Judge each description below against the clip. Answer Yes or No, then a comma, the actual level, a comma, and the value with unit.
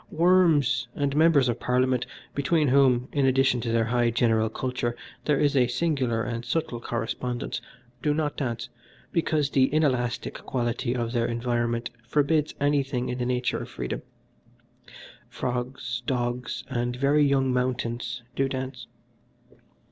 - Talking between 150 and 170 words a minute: No, average, 140 wpm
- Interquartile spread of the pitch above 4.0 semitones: No, average, 2.8 semitones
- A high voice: No, low, 125 Hz